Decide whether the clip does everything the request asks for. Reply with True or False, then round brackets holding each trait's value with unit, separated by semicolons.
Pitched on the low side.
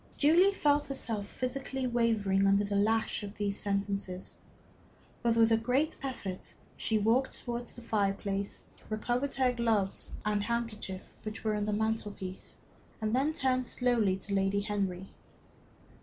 False (220 Hz)